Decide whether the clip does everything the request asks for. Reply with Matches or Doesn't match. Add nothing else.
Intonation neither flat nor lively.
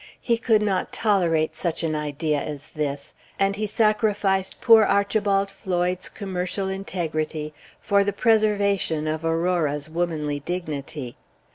Matches